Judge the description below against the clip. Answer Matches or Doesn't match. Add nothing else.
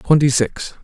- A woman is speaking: Doesn't match